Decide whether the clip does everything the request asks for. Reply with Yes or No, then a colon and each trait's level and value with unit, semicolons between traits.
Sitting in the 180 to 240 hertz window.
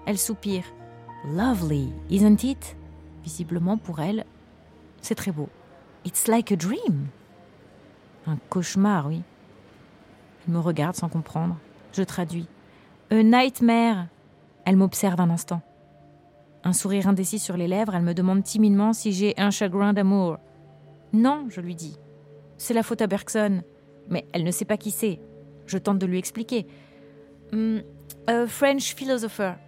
Yes: medium, 185 Hz